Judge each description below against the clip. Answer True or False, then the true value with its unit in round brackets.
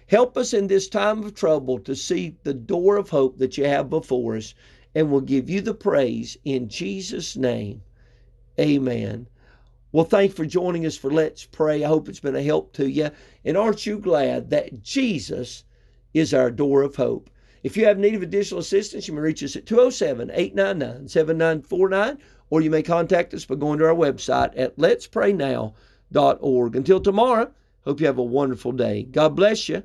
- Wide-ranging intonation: True (7.3 semitones)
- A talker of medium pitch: True (155 Hz)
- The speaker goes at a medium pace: True (185 wpm)